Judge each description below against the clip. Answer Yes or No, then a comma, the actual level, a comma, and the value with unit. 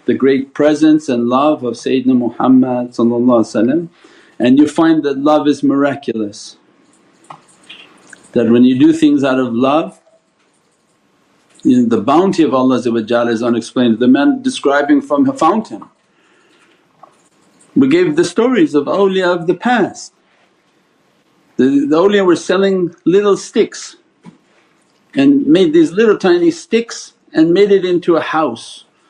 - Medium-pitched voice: Yes, medium, 155 Hz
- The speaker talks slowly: Yes, slow, 130 wpm